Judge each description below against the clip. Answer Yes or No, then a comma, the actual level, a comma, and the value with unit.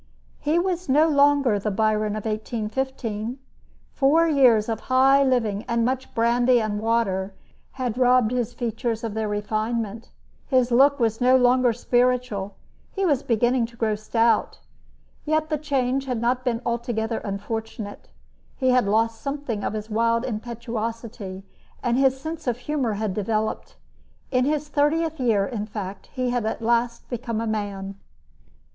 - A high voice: Yes, high, 235 Hz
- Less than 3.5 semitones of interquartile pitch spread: Yes, average, 3.1 semitones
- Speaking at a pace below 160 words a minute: Yes, average, 150 wpm